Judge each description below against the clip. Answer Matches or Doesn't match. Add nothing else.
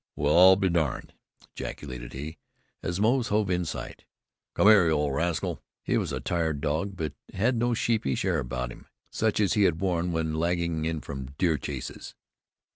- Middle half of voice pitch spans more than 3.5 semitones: Matches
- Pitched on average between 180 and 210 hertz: Doesn't match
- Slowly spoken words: Doesn't match